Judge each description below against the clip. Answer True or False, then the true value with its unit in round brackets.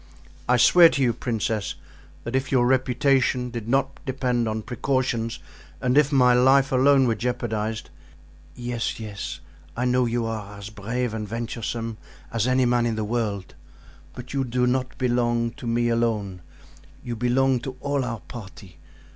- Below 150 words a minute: False (160 wpm)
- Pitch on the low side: True (120 Hz)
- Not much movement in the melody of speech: True (2.2 semitones)